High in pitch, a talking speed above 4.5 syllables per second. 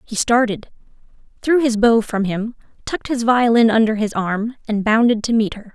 Yes: high, 225 Hz; 5.0 syllables/s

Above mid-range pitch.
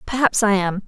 Yes: high, 210 Hz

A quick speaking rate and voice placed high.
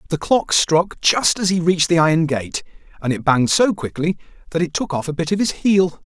No: fast, 235 wpm; medium, 165 Hz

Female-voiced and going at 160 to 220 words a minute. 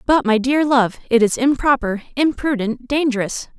No: female; average, 150 wpm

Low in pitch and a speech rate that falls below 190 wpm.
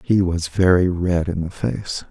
No: very low, 90 Hz; average, 200 wpm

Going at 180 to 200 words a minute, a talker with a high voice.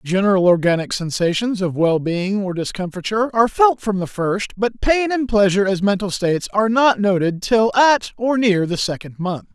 Yes: average, 190 wpm; high, 200 Hz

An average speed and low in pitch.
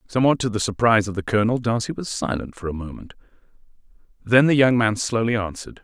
Yes: average, 195 wpm; low, 110 Hz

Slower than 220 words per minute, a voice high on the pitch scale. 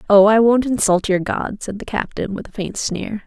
No: fast, 240 wpm; high, 210 Hz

